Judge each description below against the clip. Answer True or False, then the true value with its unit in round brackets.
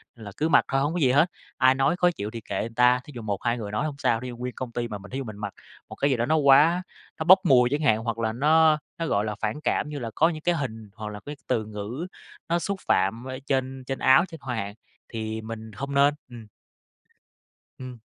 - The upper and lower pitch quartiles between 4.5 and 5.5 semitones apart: True (4.8 semitones)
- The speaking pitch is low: True (125 Hz)